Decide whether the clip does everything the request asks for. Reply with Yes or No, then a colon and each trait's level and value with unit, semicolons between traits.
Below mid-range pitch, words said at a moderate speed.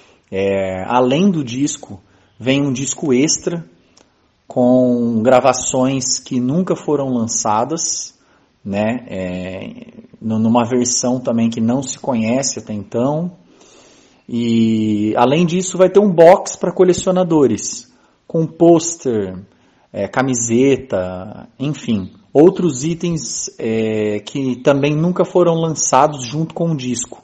No: low, 130 Hz; slow, 110 wpm